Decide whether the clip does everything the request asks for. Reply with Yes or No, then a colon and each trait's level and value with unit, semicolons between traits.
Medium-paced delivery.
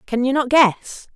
No: fast, 210 wpm